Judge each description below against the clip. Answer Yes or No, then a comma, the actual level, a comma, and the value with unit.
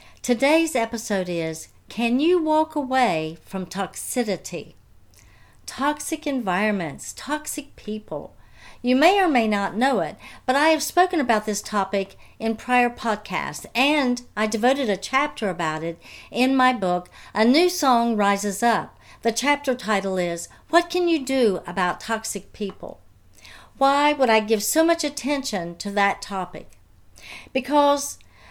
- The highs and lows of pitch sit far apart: Yes, wide, 6.4 semitones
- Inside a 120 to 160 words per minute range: Yes, average, 140 wpm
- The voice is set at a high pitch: Yes, high, 230 Hz